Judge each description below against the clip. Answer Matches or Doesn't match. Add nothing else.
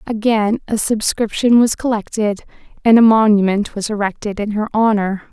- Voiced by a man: Doesn't match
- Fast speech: Doesn't match